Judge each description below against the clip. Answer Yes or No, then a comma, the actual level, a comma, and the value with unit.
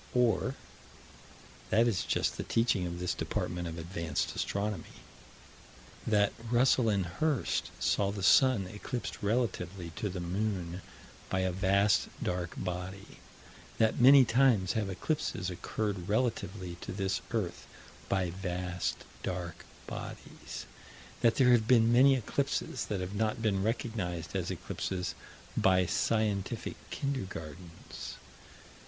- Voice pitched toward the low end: Yes, low, 100 Hz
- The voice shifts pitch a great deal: No, average, 4.0 semitones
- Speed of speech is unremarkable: No, slow, 125 wpm